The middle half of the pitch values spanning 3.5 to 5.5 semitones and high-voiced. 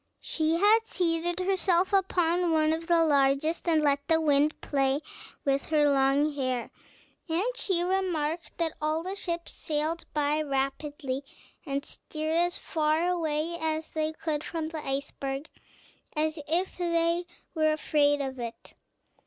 No: average, 2.8 semitones; very high, 315 Hz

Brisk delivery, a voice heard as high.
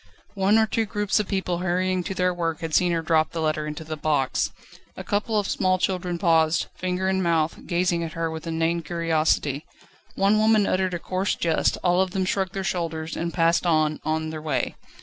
No: fast, 210 wpm; medium, 170 Hz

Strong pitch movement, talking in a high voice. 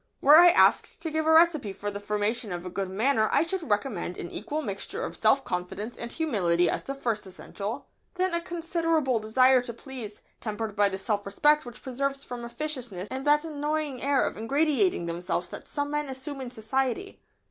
Yes: wide, 6.4 semitones; very high, 255 Hz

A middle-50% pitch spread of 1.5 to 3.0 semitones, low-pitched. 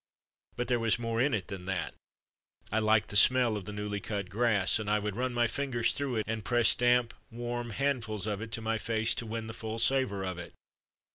Yes: narrow, 2.5 semitones; low, 110 Hz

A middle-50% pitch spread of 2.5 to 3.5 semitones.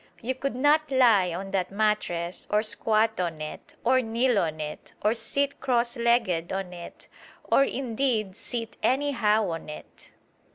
No: wide, 5.4 semitones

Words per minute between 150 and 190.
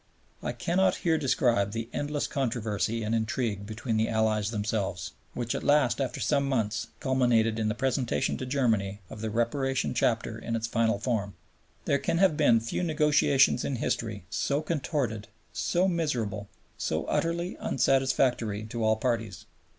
Yes: average, 155 wpm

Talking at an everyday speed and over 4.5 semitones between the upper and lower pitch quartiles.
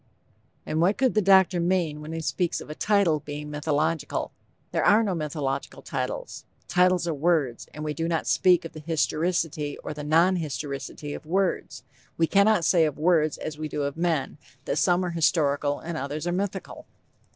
No: average, 190 wpm; average, 3.1 semitones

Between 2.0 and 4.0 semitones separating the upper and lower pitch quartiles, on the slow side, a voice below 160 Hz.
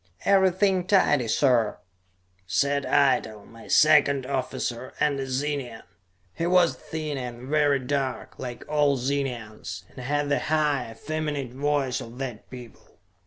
Yes: average, 3.1 semitones; slow, 130 wpm; medium, 140 Hz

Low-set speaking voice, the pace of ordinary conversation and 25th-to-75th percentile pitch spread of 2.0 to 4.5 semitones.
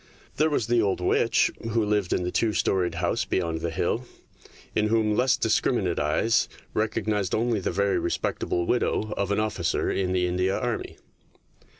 Yes: low, 105 Hz; average, 170 wpm; average, 3.8 semitones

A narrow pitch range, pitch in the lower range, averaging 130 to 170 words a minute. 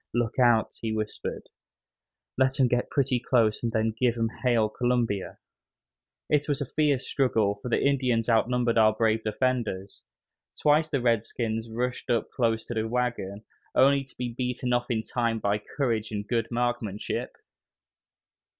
Yes: narrow, 2.2 semitones; low, 120 Hz; average, 155 wpm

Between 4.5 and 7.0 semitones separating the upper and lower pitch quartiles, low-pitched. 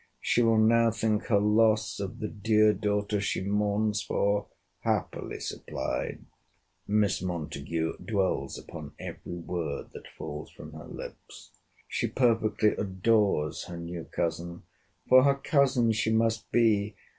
No: average, 3.2 semitones; low, 105 Hz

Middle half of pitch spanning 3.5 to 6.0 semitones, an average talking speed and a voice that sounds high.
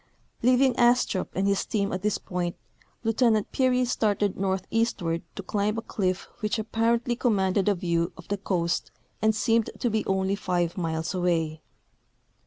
Yes: average, 3.8 semitones; average, 160 wpm; high, 200 Hz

